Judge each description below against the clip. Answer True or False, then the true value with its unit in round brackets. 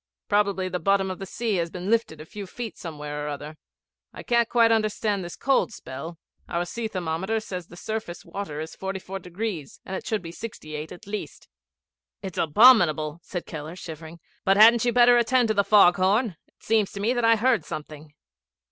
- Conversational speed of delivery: True (190 wpm)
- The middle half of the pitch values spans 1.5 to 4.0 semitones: False (5.0 semitones)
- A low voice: False (190 Hz)